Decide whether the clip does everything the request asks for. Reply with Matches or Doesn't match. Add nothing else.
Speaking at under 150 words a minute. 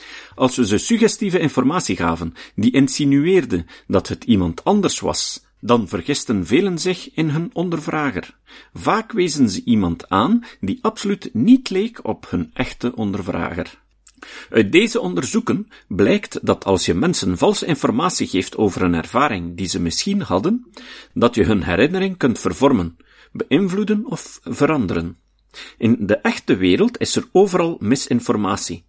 Matches